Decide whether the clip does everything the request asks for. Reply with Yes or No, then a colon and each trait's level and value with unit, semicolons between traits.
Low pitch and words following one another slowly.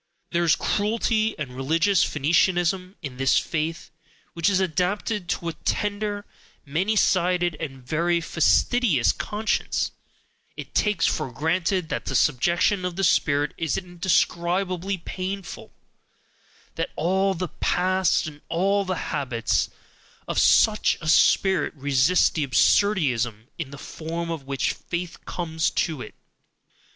No: medium, 170 Hz; slow, 130 wpm